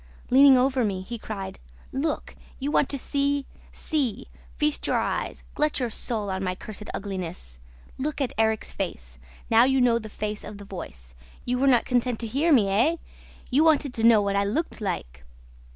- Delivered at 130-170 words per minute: No, average, 185 wpm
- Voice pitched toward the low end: No, high, 230 Hz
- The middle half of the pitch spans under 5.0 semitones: No, average, 5.3 semitones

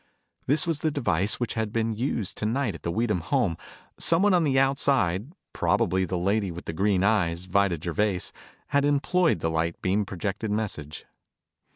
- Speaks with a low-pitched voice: Yes, low, 105 Hz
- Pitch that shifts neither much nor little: No, wide, 7.2 semitones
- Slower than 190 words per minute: Yes, average, 170 wpm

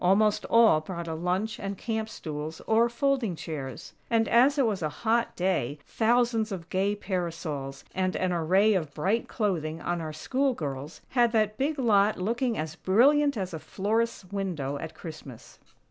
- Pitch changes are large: Yes, wide, 6.0 semitones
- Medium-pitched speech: No, high, 195 Hz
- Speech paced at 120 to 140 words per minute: No, average, 170 wpm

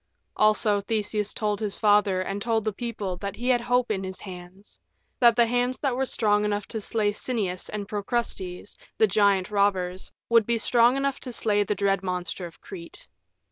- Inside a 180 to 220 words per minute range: Yes, average, 185 wpm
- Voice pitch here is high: Yes, high, 210 Hz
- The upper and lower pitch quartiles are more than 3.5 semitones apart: No, average, 3.0 semitones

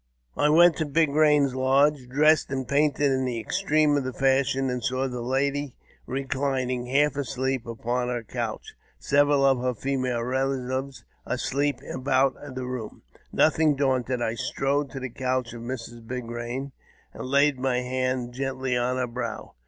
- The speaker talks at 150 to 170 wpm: Yes, average, 165 wpm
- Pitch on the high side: No, low, 130 Hz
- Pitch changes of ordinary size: No, narrow, 2.0 semitones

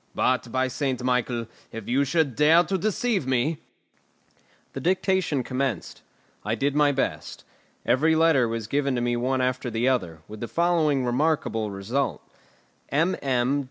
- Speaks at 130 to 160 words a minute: Yes, average, 150 wpm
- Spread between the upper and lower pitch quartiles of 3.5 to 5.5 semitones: Yes, average, 4.1 semitones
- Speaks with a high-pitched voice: No, low, 130 Hz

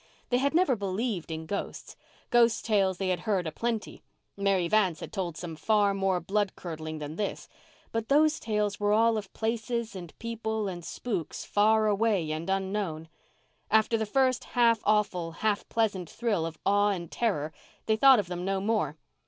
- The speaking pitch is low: No, high, 205 Hz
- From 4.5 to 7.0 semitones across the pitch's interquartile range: No, average, 3.9 semitones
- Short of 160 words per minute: No, average, 175 wpm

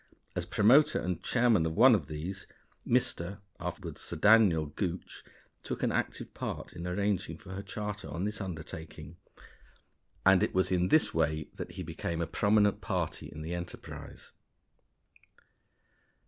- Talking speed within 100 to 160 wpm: Yes, average, 145 wpm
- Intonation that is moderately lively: Yes, average, 4.1 semitones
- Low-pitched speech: Yes, very low, 95 Hz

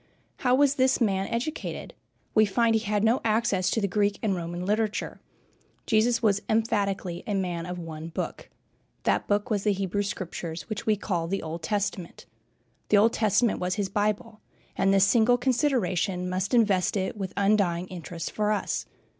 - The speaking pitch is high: Yes, high, 200 Hz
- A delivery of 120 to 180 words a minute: Yes, average, 170 wpm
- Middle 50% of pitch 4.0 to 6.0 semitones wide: No, average, 3.2 semitones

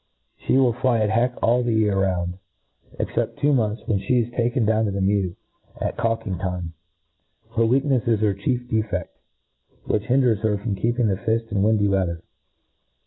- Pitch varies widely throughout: No, average, 3.4 semitones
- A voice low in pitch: Yes, low, 110 Hz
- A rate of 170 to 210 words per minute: Yes, average, 175 wpm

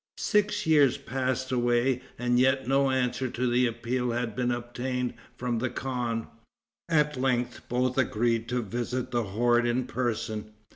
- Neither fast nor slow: Yes, average, 150 wpm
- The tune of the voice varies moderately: No, narrow, 1.4 semitones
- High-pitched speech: No, low, 125 Hz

